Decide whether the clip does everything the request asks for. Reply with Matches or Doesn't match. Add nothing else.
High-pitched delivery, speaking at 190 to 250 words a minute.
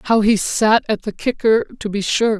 Matches